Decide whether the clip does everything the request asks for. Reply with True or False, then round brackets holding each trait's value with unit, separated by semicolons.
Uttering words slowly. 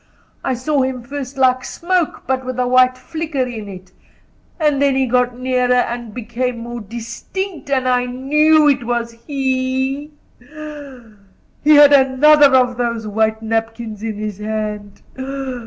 False (150 wpm)